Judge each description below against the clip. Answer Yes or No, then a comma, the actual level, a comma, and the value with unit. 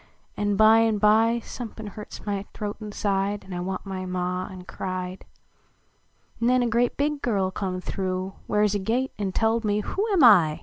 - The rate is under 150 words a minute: No, average, 185 wpm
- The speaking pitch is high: Yes, high, 205 Hz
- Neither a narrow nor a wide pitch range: Yes, average, 3.1 semitones